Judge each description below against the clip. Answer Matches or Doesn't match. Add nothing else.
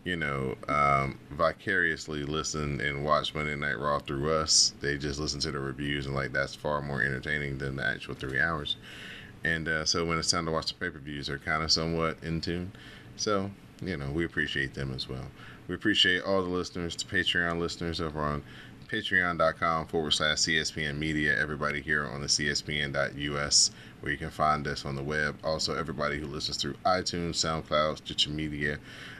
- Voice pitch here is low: Matches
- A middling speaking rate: Matches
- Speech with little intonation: Matches